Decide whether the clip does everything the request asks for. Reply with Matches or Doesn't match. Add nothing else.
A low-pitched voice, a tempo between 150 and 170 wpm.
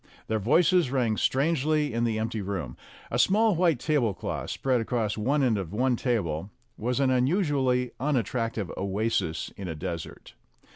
Matches